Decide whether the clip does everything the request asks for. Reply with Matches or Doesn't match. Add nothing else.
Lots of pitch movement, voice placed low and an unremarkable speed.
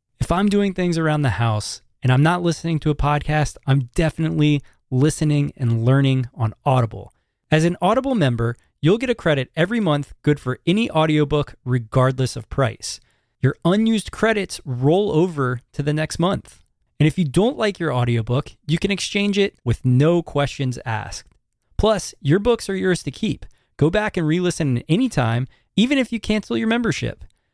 Doesn't match